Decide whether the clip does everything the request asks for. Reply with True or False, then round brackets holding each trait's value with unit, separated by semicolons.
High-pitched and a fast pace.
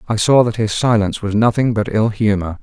False (110 Hz; 230 wpm)